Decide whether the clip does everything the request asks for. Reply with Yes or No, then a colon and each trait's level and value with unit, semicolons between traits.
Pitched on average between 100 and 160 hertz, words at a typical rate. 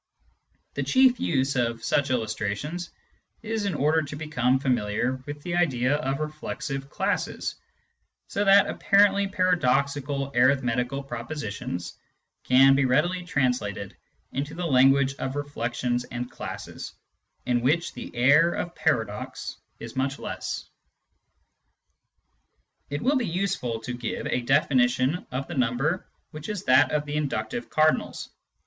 No: medium, 140 Hz; slow, 130 wpm